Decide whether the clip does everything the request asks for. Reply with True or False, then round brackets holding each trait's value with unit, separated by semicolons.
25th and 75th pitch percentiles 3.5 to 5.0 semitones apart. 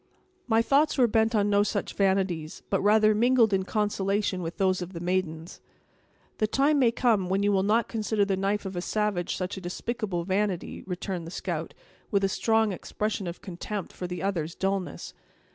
False (2.8 semitones)